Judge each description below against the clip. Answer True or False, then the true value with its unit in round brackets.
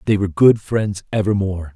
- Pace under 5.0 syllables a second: False (5.9 syllables/s)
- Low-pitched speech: True (100 Hz)